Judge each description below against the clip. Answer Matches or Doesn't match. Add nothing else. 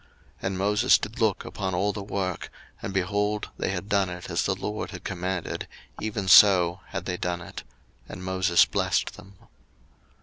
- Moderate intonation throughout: Doesn't match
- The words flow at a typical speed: Matches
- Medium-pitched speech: Doesn't match